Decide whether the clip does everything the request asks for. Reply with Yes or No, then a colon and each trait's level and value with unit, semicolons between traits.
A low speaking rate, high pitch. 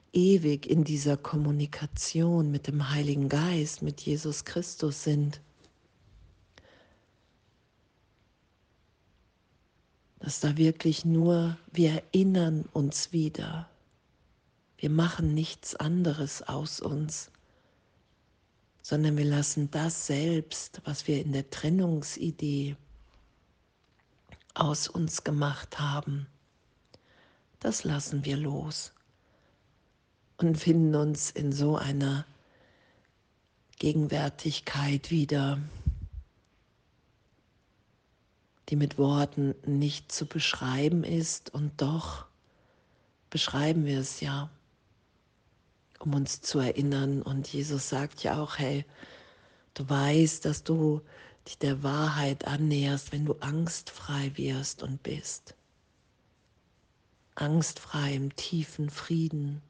No: slow, 95 wpm; medium, 145 Hz